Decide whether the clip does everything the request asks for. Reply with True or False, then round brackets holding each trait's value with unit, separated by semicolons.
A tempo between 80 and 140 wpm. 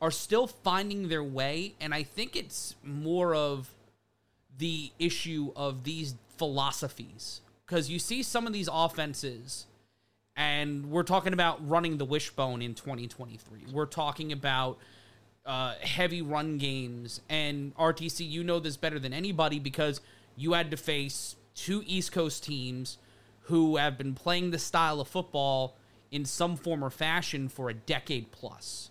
False (155 wpm)